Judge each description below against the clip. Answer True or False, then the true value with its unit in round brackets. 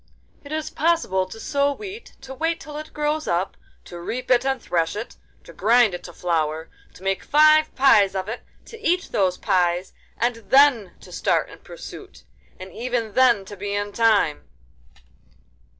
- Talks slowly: False (170 wpm)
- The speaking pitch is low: False (230 Hz)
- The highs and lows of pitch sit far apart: True (7.5 semitones)